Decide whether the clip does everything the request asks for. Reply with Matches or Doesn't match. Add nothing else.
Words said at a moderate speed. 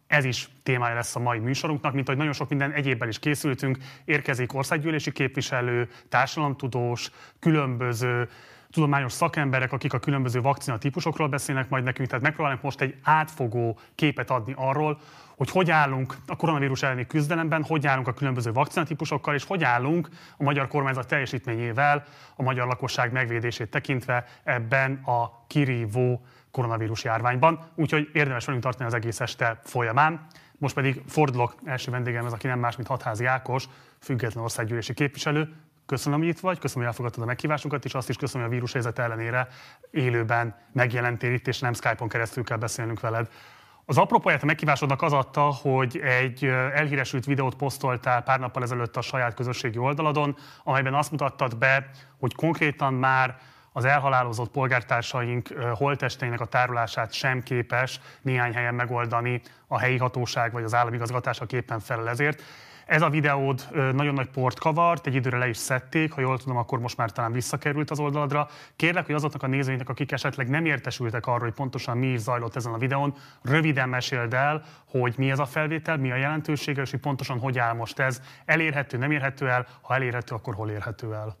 Doesn't match